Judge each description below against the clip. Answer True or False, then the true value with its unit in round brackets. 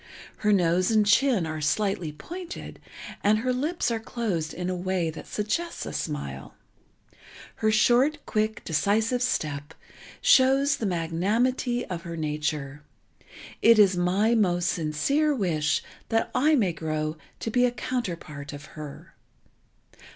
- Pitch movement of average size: False (7.0 semitones)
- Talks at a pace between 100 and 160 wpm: True (135 wpm)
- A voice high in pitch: True (195 Hz)